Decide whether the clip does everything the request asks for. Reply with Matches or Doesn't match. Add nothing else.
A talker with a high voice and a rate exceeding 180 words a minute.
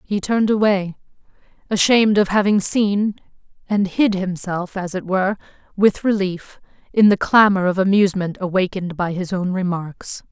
Doesn't match